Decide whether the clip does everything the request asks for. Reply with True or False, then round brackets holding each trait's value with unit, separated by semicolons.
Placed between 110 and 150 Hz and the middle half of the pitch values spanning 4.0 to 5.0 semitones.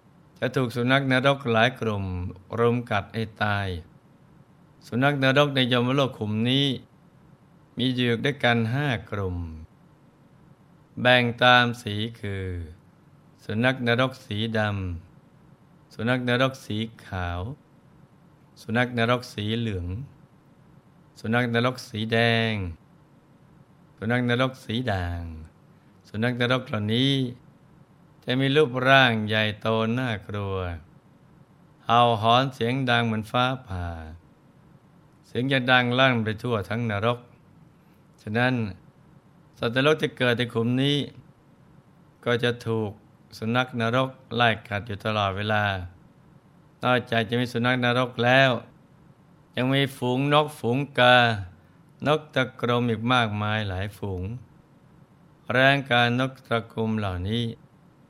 True (125 Hz; 4.4 semitones)